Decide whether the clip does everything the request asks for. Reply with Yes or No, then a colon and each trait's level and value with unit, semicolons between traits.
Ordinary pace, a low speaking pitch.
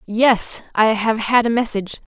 No: average, 170 wpm; high, 225 Hz